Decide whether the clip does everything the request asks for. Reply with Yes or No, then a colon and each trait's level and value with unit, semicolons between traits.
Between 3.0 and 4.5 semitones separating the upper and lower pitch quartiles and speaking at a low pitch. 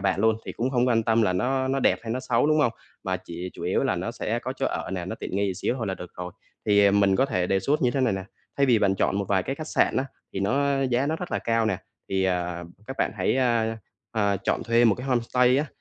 No: average, 5.0 semitones; low, 115 Hz